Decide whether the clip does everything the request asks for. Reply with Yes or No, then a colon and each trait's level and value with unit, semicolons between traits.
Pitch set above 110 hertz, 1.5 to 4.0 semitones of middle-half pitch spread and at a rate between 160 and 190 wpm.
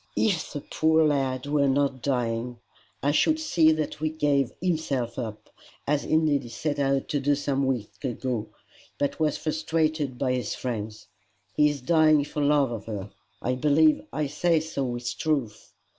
Yes: medium, 140 Hz; average, 3.6 semitones; average, 170 wpm